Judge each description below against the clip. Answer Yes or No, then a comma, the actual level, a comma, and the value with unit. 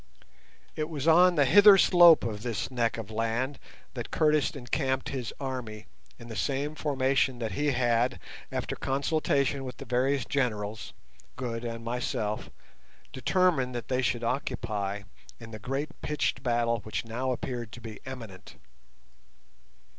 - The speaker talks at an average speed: Yes, average, 145 wpm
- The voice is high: No, low, 125 Hz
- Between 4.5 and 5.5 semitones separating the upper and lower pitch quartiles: No, average, 3.3 semitones